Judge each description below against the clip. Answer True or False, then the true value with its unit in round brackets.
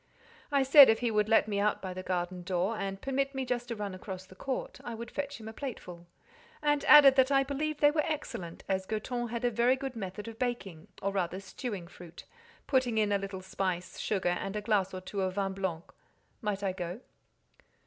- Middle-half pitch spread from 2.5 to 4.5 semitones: False (5.1 semitones)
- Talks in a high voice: True (210 Hz)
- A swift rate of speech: True (215 wpm)